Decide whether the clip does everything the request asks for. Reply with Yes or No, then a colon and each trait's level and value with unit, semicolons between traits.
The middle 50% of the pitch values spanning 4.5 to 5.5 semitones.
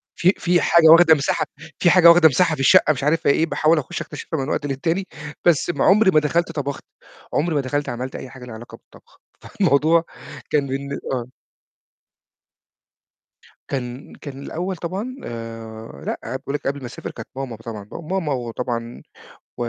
Yes: average, 4.8 semitones